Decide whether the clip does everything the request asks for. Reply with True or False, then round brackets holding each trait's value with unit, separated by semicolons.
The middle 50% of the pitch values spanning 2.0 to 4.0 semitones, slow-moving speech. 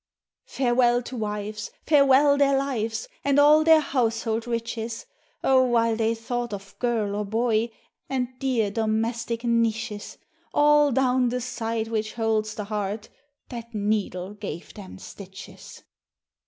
True (2.7 semitones; 130 wpm)